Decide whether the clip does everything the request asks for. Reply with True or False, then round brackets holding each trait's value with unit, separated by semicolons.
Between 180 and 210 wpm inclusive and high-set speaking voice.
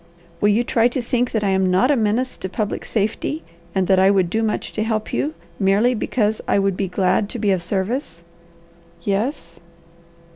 True (195 wpm; 205 Hz)